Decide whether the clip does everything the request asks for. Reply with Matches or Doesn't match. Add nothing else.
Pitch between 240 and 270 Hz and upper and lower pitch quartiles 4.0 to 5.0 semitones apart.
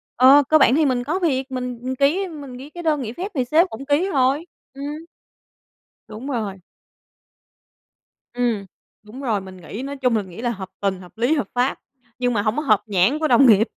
Matches